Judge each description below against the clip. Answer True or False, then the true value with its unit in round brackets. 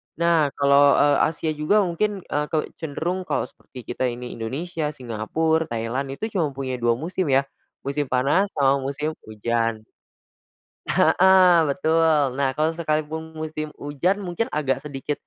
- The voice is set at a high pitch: False (150 Hz)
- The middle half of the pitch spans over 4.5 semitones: False (3.5 semitones)